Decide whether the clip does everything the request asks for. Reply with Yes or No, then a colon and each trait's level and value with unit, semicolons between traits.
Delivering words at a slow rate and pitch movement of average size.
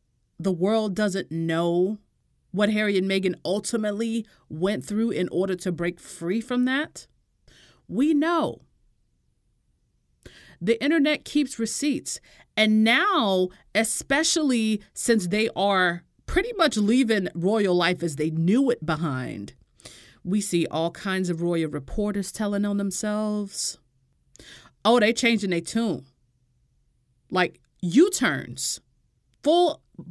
Yes: slow, 115 wpm; average, 4.9 semitones